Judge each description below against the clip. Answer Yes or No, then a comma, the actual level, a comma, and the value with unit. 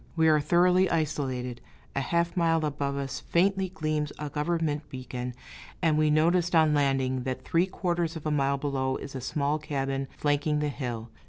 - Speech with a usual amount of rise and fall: Yes, average, 3.3 semitones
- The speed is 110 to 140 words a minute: No, average, 175 wpm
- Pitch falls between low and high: Yes, medium, 150 Hz